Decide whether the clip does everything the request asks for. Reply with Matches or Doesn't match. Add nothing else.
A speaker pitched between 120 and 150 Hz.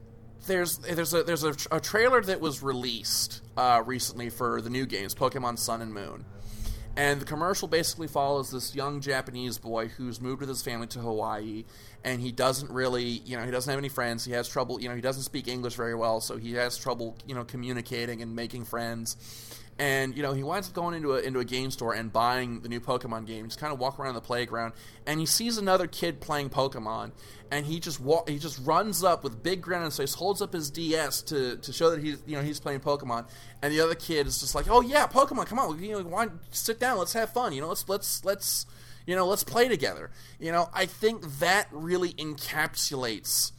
Matches